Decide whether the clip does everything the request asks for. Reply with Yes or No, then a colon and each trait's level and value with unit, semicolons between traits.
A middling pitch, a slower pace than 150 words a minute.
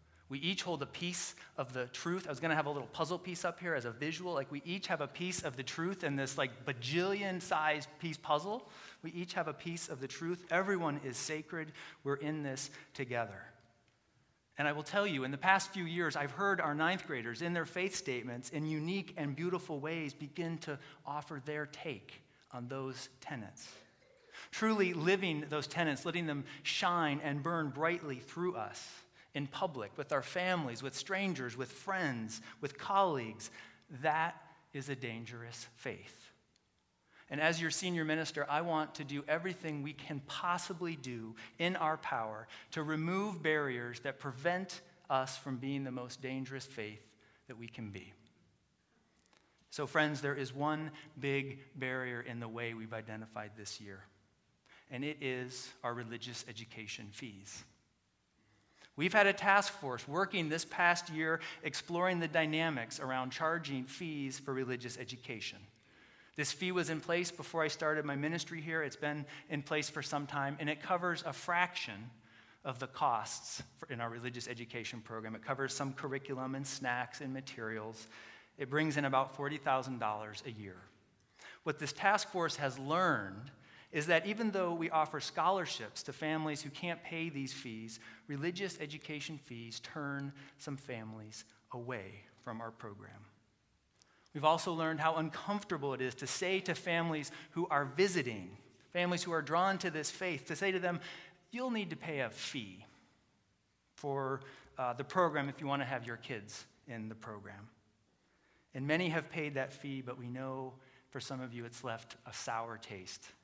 No: medium, 145 Hz; average, 170 wpm